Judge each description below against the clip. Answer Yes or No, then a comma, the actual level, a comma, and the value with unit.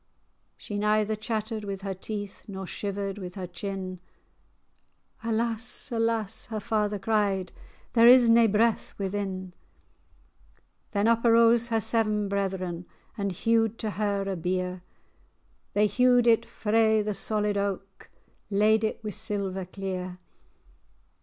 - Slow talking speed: Yes, slow, 130 wpm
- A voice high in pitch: Yes, high, 210 Hz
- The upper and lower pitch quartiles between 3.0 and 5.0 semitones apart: No, narrow, 2.5 semitones